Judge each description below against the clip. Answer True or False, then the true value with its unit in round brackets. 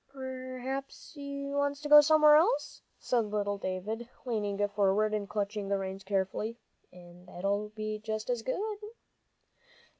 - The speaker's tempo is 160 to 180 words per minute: False (140 wpm)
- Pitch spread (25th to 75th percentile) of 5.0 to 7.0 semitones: True (5.3 semitones)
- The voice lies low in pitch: False (215 Hz)